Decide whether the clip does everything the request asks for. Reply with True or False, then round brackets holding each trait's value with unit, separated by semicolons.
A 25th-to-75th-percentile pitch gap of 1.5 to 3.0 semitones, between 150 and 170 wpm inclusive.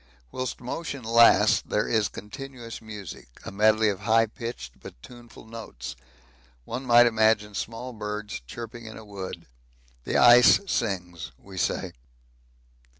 False (2.4 semitones; 135 wpm)